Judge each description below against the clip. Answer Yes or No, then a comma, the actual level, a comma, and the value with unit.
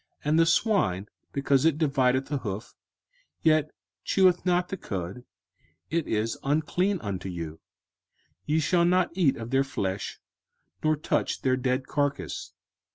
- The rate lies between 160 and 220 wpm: No, average, 145 wpm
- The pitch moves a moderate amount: No, wide, 6.5 semitones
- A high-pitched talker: No, medium, 140 Hz